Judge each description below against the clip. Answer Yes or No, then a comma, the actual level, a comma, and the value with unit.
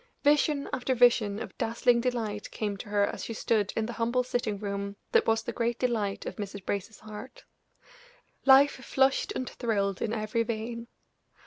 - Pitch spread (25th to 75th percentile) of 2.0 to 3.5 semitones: Yes, average, 2.9 semitones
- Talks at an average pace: Yes, average, 175 wpm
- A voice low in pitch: No, high, 225 Hz